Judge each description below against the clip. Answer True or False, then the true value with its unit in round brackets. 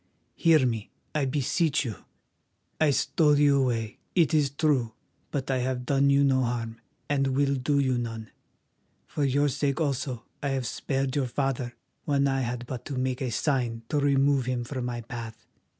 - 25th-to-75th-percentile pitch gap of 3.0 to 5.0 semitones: False (2.6 semitones)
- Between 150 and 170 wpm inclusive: False (180 wpm)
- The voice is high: False (135 Hz)